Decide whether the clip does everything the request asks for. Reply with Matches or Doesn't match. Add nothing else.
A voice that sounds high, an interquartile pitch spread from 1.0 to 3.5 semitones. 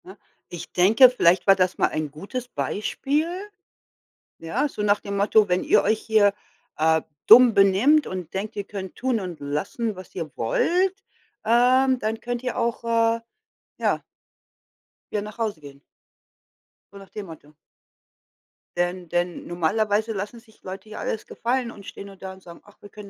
Doesn't match